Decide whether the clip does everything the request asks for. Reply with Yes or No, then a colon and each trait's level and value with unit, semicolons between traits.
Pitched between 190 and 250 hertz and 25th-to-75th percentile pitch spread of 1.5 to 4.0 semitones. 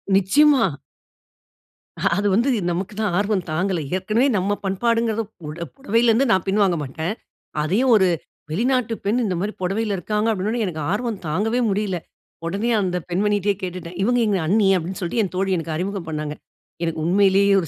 Yes: high, 195 Hz; average, 3.4 semitones